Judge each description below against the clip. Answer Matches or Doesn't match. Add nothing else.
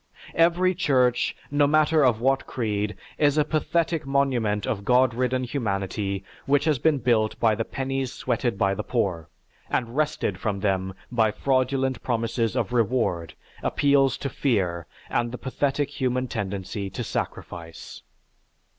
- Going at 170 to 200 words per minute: Doesn't match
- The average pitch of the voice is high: Doesn't match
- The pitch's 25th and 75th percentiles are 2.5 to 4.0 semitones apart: Doesn't match